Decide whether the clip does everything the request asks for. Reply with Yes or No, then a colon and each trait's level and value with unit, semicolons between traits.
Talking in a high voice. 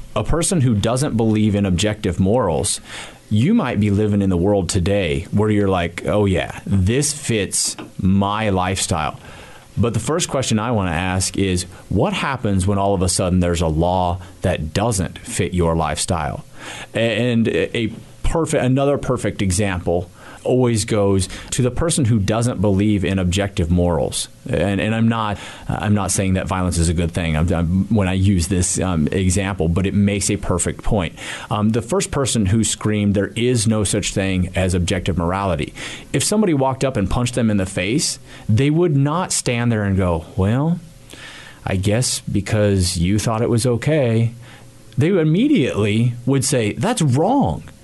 No: low, 105 Hz